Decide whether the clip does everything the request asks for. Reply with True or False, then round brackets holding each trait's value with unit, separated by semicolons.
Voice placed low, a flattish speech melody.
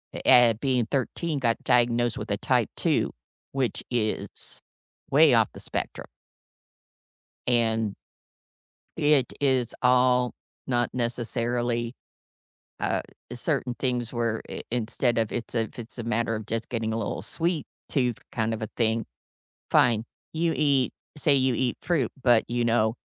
True (120 Hz; 2.0 semitones)